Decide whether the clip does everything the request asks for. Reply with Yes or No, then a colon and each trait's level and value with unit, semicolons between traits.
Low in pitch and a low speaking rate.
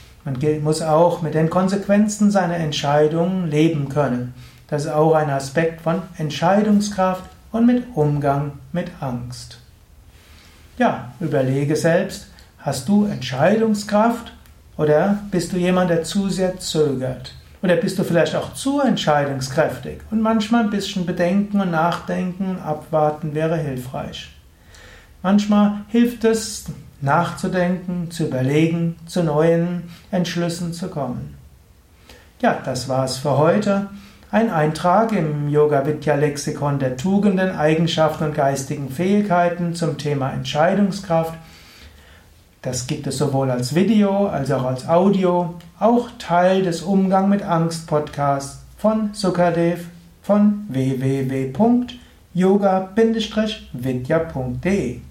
No: medium, 165 Hz; slow, 110 wpm